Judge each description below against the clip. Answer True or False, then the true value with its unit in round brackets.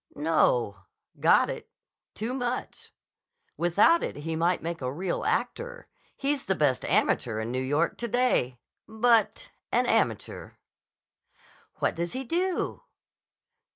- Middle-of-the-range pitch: True (175 Hz)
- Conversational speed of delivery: False (120 wpm)